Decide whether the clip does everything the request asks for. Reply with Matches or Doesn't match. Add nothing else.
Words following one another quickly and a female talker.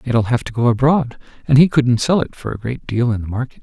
Doesn't match